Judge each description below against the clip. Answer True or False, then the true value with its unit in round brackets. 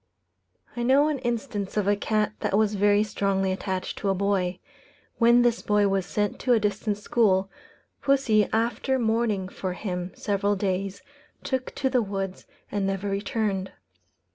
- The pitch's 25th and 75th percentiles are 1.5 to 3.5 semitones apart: True (2.9 semitones)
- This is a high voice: True (205 Hz)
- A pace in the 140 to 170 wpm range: True (160 wpm)